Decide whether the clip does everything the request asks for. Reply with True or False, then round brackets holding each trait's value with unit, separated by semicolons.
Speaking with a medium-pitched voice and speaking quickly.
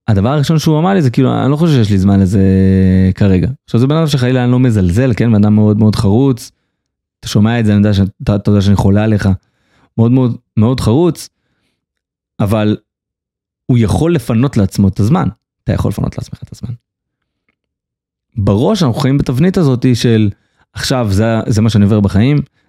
False (115 Hz; 185 wpm)